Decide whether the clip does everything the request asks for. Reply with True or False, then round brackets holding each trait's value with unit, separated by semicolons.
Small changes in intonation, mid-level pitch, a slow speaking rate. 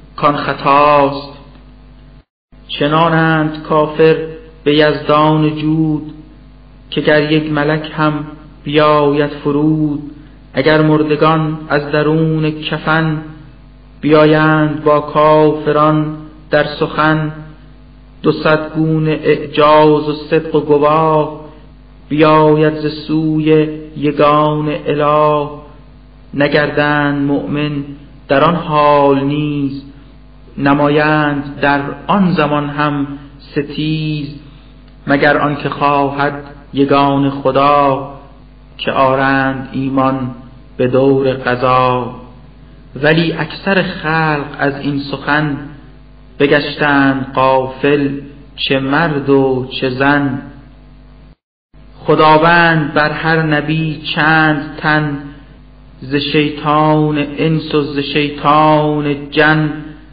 True (1.5 semitones; 150 Hz; 85 wpm)